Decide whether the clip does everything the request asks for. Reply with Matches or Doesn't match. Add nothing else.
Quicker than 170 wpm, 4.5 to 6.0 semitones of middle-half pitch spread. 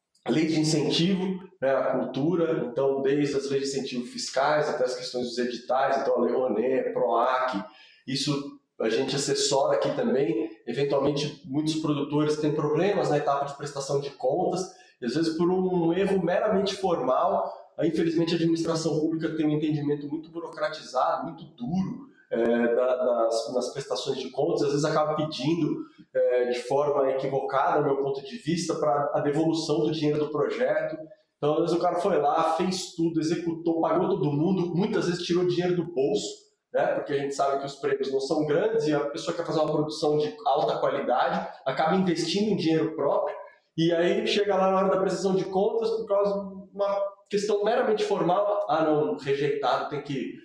Matches